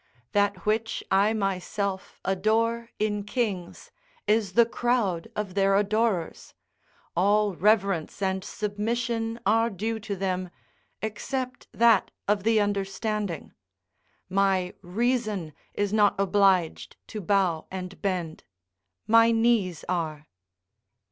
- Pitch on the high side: Yes, high, 205 Hz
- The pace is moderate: No, slow, 110 wpm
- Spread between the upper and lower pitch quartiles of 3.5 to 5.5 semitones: No, average, 2.9 semitones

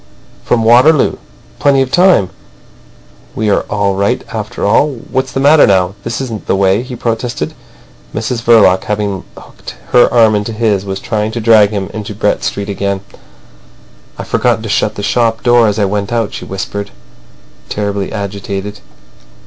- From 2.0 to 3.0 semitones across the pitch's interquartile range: Yes, average, 2.7 semitones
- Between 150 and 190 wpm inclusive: Yes, average, 165 wpm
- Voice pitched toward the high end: No, low, 105 Hz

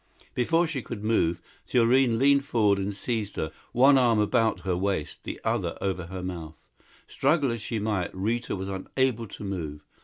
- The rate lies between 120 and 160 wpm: No, average, 175 wpm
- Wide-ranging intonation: No, average, 4.6 semitones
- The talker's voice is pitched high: No, low, 105 Hz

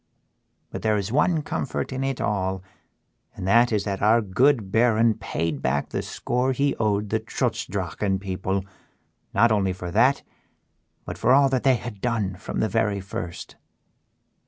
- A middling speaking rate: Yes, average, 165 wpm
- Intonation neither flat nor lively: Yes, average, 4.1 semitones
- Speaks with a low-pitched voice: Yes, low, 110 Hz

